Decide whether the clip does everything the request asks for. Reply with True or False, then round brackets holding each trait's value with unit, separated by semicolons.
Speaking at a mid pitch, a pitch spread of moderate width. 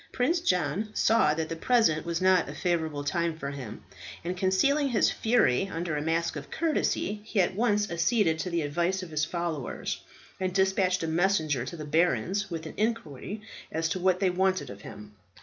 True (175 Hz; 3.8 semitones)